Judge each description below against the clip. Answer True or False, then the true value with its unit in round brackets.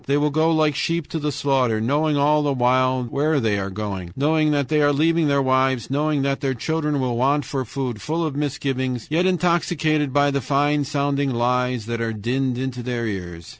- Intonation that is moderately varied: True (3.1 semitones)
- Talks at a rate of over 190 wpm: True (205 wpm)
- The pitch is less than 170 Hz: True (140 Hz)